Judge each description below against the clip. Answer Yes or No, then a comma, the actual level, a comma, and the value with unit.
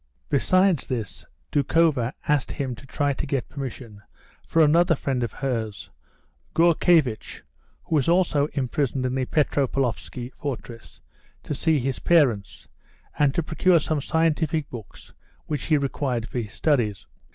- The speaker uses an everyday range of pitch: Yes, average, 4.2 semitones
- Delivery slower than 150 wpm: Yes, average, 140 wpm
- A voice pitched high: No, medium, 140 Hz